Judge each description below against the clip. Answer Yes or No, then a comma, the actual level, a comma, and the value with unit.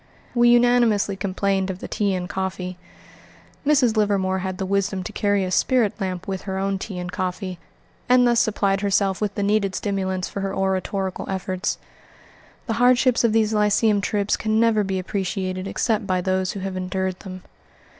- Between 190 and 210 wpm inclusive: No, average, 175 wpm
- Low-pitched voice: No, high, 195 Hz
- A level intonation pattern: Yes, narrow, 2.2 semitones